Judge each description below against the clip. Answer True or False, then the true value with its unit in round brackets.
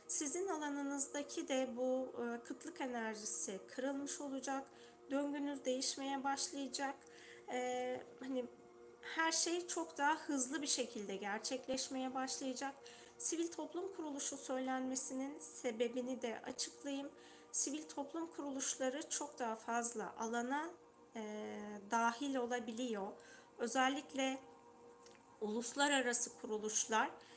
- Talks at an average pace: False (90 wpm)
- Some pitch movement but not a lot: True (3.2 semitones)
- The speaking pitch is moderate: False (260 Hz)